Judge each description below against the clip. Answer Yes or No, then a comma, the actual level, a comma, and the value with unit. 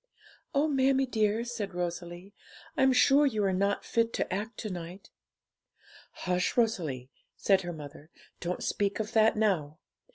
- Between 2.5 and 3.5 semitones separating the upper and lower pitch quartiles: No, average, 4.6 semitones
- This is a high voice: Yes, high, 200 Hz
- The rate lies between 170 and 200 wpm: No, average, 150 wpm